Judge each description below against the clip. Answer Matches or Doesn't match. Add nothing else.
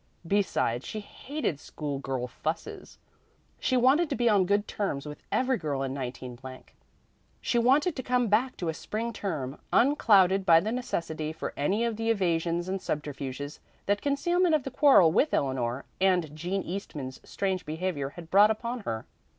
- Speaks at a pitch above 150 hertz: Matches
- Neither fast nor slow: Matches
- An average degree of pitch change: Doesn't match